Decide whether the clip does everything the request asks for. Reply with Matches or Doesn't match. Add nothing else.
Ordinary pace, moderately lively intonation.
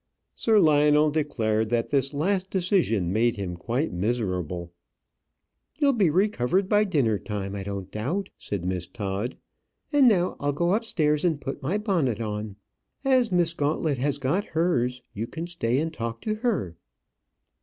Doesn't match